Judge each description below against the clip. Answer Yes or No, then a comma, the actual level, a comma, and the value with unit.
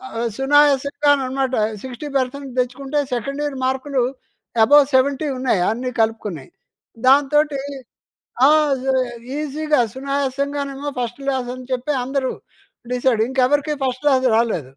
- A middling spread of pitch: No, narrow, 2.0 semitones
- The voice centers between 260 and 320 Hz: Yes, very high, 270 Hz